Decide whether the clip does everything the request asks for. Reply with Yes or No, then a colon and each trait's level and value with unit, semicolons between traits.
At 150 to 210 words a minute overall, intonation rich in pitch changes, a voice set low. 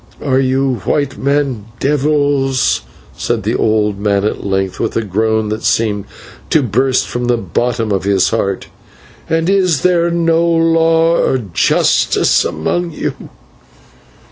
No: average, 140 wpm; wide, 6.7 semitones; low, 130 Hz